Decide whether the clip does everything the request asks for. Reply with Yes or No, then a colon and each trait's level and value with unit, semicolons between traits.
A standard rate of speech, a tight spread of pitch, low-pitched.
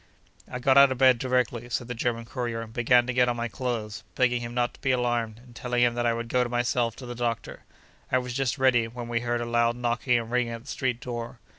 No: fast, 260 wpm; narrow, 1.0 semitones; low, 120 Hz